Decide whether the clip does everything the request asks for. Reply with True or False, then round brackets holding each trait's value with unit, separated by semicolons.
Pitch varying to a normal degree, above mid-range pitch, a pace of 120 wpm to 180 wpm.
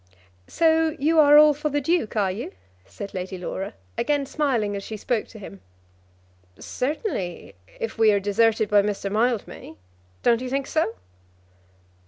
False (6.4 semitones; 230 Hz; 155 wpm)